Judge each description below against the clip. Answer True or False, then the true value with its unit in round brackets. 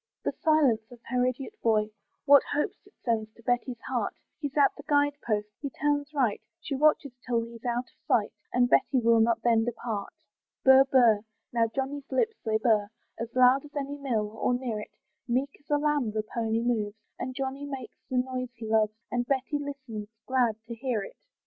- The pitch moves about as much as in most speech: True (3.5 semitones)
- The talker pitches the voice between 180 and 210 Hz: False (245 Hz)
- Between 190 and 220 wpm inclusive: True (195 wpm)